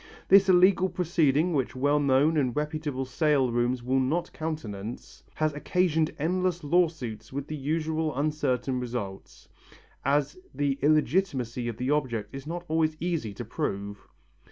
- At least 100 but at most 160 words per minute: Yes, average, 140 wpm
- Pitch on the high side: No, medium, 145 Hz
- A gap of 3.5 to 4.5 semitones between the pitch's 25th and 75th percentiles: Yes, average, 4.0 semitones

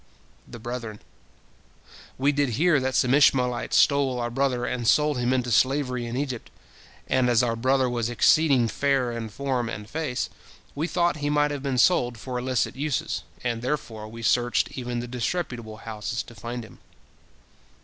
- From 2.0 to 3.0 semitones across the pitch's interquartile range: Yes, average, 2.7 semitones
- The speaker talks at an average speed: Yes, average, 170 wpm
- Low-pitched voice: Yes, low, 125 Hz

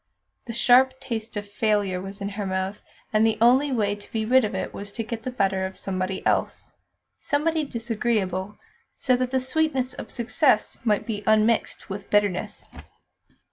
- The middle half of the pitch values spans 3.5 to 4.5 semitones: Yes, average, 3.8 semitones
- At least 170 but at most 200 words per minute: Yes, average, 175 wpm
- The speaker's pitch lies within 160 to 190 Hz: No, high, 220 Hz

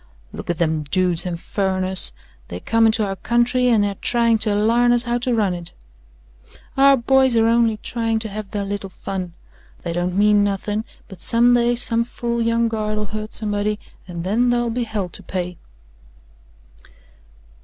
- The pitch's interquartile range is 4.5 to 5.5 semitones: No, average, 3.5 semitones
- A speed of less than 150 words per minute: No, average, 170 wpm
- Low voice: No, high, 215 Hz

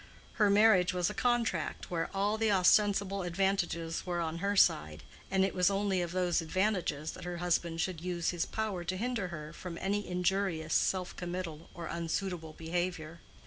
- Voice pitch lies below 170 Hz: No, medium, 180 Hz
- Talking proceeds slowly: No, average, 175 wpm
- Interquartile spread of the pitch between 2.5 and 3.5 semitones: Yes, average, 2.8 semitones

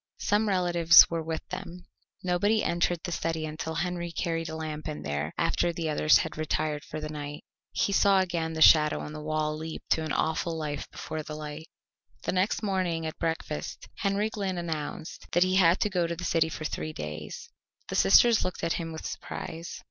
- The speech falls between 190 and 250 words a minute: Yes, average, 200 wpm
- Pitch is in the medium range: Yes, medium, 165 Hz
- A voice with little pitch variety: Yes, narrow, 2.3 semitones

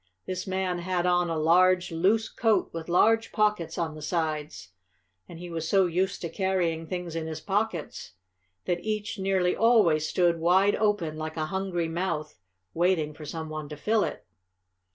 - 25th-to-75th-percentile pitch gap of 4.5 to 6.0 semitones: No, average, 2.9 semitones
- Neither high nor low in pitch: Yes, medium, 175 Hz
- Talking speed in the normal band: Yes, average, 175 wpm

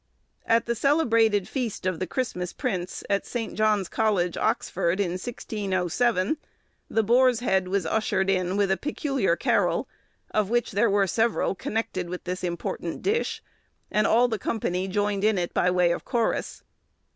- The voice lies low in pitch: No, high, 205 Hz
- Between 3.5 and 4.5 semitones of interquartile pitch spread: Yes, average, 4.1 semitones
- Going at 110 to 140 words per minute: No, average, 160 wpm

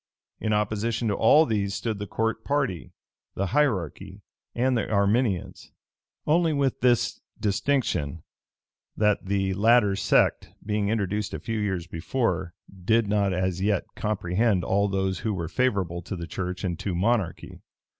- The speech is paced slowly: No, average, 145 wpm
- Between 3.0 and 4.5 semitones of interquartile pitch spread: Yes, average, 3.3 semitones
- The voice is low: Yes, low, 100 Hz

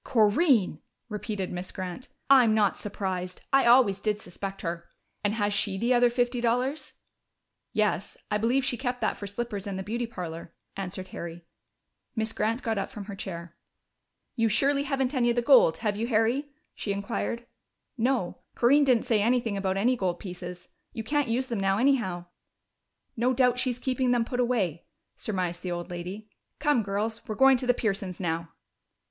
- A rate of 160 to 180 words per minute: Yes, average, 175 wpm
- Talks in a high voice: Yes, high, 220 Hz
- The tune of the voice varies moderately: Yes, average, 4.4 semitones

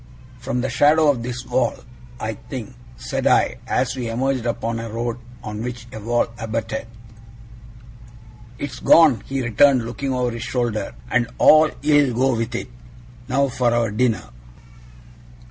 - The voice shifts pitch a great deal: No, narrow, 2.4 semitones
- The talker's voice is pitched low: Yes, low, 120 Hz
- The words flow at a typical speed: Yes, average, 150 wpm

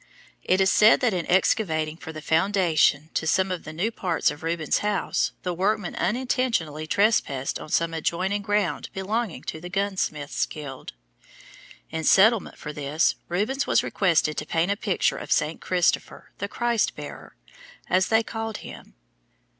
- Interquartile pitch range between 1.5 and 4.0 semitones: No, average, 4.6 semitones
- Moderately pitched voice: Yes, medium, 180 Hz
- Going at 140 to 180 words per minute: Yes, average, 160 wpm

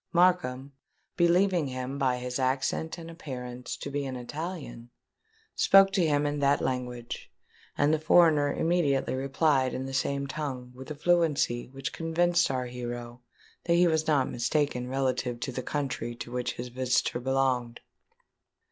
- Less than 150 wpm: No, average, 155 wpm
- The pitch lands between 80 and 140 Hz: Yes, low, 135 Hz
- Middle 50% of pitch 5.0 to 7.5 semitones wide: No, average, 3.9 semitones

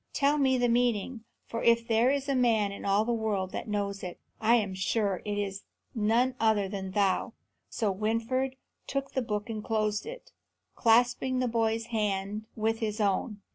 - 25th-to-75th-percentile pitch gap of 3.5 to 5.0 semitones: No, average, 2.8 semitones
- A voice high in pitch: Yes, high, 220 Hz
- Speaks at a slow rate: No, average, 180 wpm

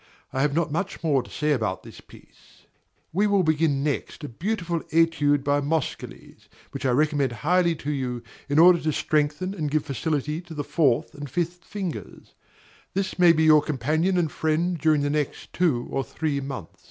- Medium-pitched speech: Yes, medium, 155 Hz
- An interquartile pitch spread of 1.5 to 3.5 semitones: Yes, average, 2.9 semitones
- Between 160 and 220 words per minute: Yes, average, 185 wpm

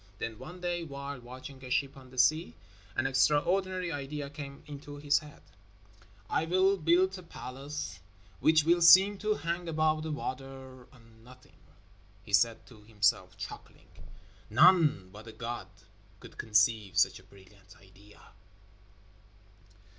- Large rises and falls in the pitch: Yes, wide, 5.9 semitones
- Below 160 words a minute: Yes, average, 140 wpm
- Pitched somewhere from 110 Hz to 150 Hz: Yes, medium, 140 Hz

